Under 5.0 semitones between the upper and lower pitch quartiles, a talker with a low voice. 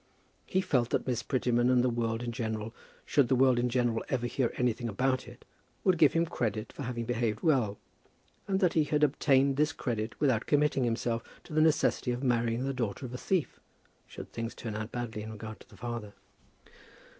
Yes: average, 2.9 semitones; low, 120 Hz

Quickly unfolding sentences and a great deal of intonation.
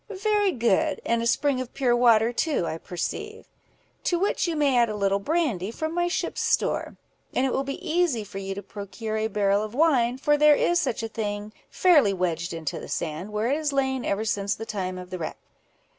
Yes: fast, 220 wpm; wide, 6.7 semitones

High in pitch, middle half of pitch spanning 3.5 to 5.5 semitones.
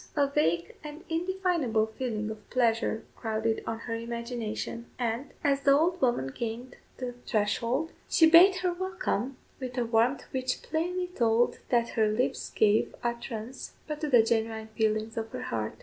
Yes: high, 235 Hz; average, 4.3 semitones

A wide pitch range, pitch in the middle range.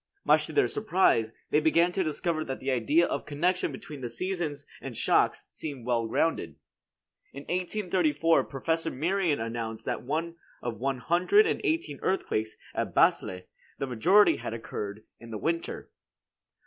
Yes: wide, 6.8 semitones; medium, 150 Hz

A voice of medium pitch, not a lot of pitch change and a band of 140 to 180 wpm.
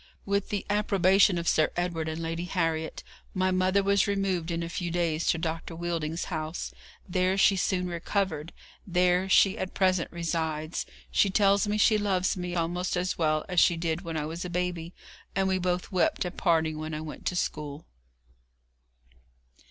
Yes: medium, 175 Hz; narrow, 2.3 semitones; average, 175 wpm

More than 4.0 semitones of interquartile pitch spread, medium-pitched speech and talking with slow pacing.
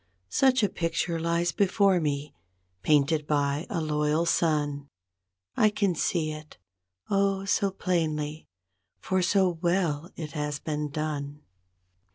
No: average, 3.6 semitones; medium, 160 Hz; slow, 125 wpm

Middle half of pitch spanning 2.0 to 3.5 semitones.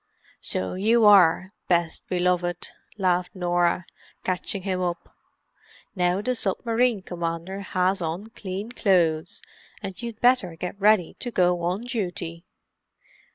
Yes: average, 2.8 semitones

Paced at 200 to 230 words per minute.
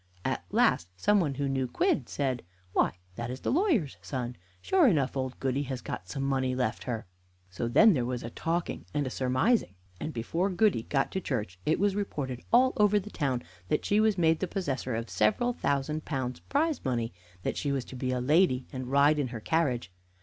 Yes: fast, 205 wpm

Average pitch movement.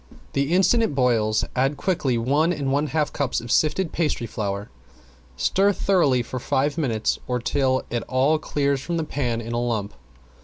Yes: average, 4.4 semitones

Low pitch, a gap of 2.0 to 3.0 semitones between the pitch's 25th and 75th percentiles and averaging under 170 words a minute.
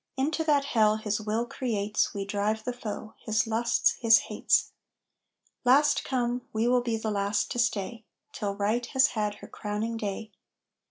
No: high, 220 Hz; narrow, 2.5 semitones; average, 160 wpm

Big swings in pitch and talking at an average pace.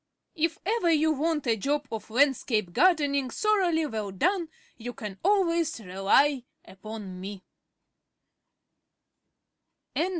No: wide, 7.5 semitones; slow, 105 wpm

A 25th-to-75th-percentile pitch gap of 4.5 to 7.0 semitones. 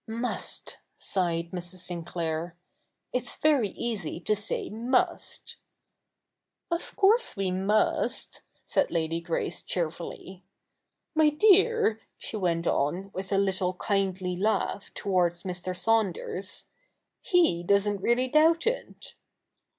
Yes: average, 5.1 semitones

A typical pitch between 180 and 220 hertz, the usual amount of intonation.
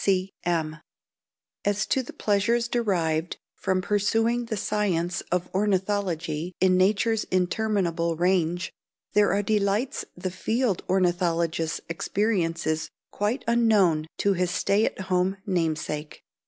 Yes: medium, 185 Hz; average, 3.3 semitones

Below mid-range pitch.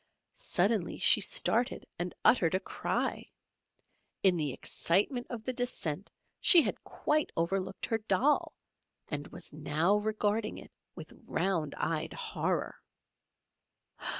No: high, 195 Hz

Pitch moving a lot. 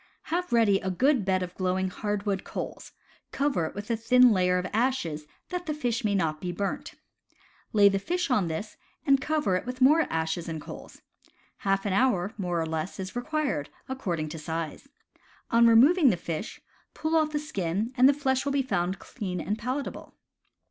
Yes: wide, 6.5 semitones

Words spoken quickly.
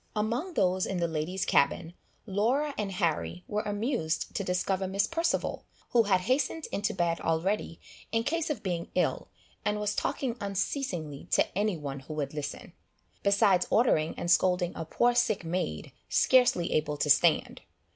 No: average, 160 wpm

